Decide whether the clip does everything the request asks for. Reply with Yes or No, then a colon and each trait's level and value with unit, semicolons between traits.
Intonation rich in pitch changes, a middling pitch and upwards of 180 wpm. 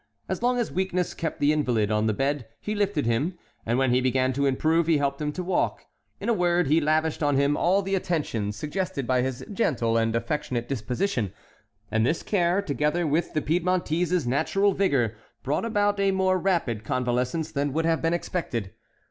Yes: wide, 6.0 semitones; medium, 150 Hz; average, 190 wpm